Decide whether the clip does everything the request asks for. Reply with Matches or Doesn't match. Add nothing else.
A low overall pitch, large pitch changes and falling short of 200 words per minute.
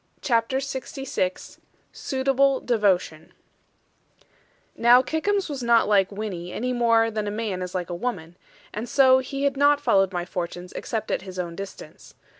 Doesn't match